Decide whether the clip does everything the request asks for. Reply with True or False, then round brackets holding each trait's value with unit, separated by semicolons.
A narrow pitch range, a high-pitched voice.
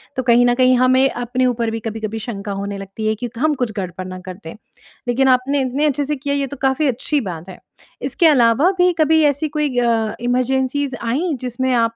False (3.8 semitones; 250 Hz)